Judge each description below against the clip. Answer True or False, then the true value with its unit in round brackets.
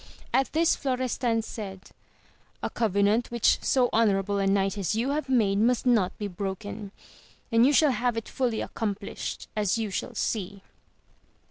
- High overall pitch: True (220 Hz)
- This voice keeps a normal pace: True (155 wpm)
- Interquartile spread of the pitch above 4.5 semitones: False (3.6 semitones)